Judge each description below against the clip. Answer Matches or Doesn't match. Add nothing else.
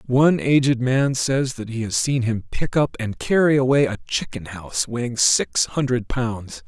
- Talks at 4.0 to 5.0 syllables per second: Matches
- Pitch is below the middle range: Matches